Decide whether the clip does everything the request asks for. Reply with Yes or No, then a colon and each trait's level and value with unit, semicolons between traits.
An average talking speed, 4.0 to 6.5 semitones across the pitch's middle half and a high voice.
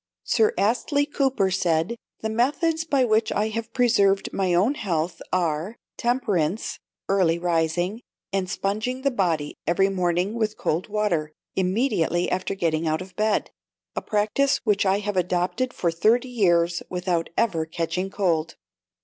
Yes: average, 145 wpm; average, 4.6 semitones; high, 195 Hz